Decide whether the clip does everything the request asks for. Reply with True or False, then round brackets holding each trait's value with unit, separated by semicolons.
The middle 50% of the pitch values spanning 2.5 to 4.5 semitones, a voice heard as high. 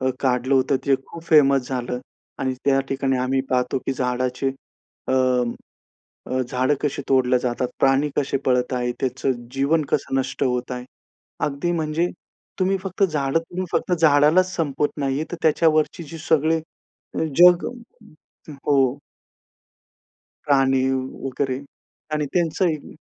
False (3.3 semitones; 135 Hz)